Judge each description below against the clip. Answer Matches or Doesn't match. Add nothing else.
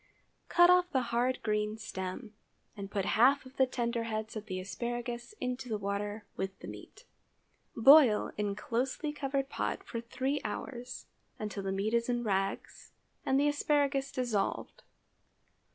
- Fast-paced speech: Doesn't match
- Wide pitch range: Doesn't match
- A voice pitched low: Doesn't match